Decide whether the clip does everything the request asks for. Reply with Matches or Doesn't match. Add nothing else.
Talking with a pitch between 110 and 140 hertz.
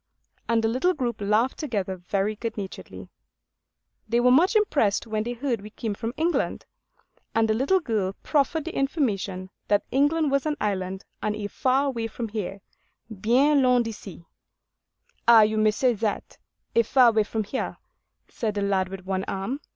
Doesn't match